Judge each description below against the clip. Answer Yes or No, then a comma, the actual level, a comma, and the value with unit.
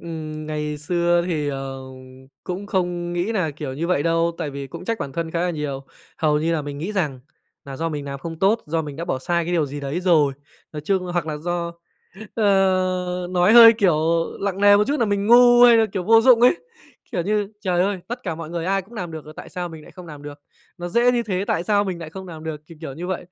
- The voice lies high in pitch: No, medium, 175 Hz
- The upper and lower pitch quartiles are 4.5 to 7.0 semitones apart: No, average, 4.0 semitones